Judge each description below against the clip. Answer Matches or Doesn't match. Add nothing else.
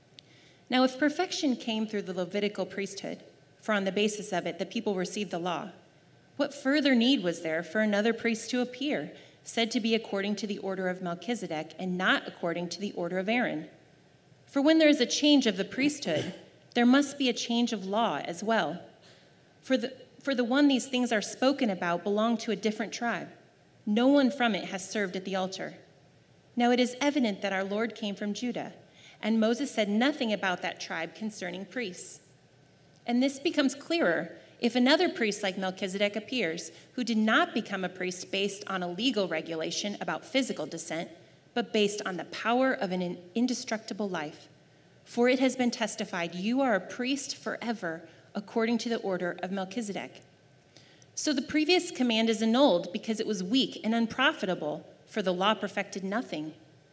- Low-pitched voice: Doesn't match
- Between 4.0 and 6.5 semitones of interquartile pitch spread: Matches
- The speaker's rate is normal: Matches